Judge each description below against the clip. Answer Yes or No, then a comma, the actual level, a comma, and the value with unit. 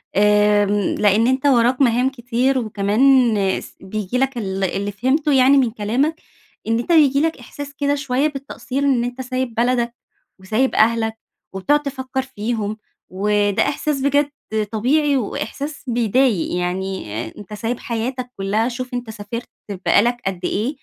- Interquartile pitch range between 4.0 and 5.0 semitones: Yes, average, 4.3 semitones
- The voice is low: No, high, 240 Hz